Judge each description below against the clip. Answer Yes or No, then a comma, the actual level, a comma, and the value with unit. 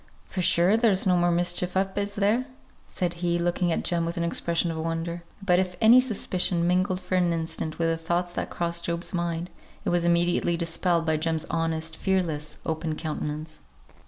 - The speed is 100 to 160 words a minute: No, average, 190 wpm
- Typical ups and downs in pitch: No, narrow, 1.8 semitones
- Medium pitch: Yes, medium, 170 Hz